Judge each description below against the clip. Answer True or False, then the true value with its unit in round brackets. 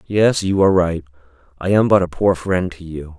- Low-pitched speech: True (90 Hz)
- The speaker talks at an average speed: False (225 wpm)